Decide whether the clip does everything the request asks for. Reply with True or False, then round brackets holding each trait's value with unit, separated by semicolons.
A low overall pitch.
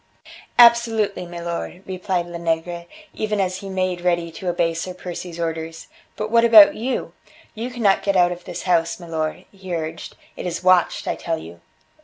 False (180 Hz)